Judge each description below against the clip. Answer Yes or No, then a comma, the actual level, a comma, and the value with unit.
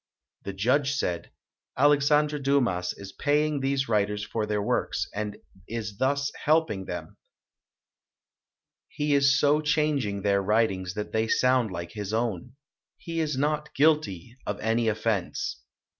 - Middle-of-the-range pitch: No, low, 115 Hz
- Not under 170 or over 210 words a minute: No, average, 145 wpm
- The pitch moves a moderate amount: No, wide, 5.8 semitones